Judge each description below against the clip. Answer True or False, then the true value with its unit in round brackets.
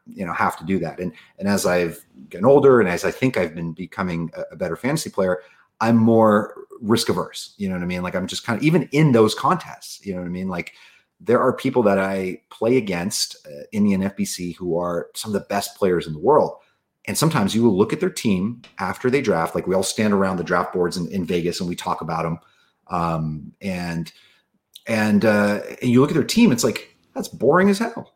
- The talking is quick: True (240 wpm)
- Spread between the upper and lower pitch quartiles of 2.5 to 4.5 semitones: False (5.1 semitones)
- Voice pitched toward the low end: True (95 Hz)